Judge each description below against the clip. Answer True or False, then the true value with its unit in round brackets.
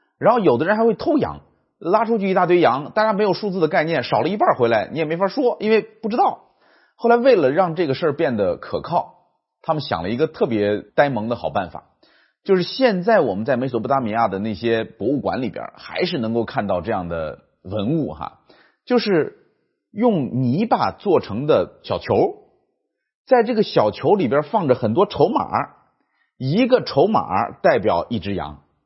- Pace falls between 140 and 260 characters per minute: False (275 characters per minute)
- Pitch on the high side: True (195 Hz)